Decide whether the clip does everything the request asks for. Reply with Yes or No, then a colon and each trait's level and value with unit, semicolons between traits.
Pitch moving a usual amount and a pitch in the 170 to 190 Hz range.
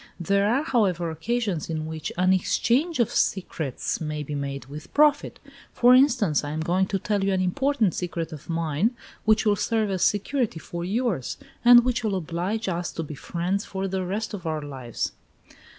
No: wide, 5.7 semitones; medium, 185 Hz